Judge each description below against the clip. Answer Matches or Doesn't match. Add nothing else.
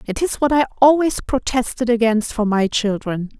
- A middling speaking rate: Matches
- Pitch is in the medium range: Doesn't match